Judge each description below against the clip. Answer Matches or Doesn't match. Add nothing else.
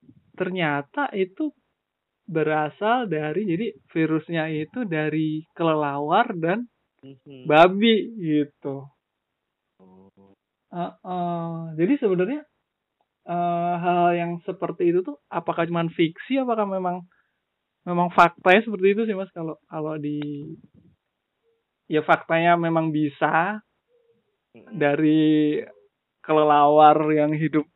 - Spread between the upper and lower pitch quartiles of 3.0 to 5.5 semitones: Matches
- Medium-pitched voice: Matches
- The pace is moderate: Matches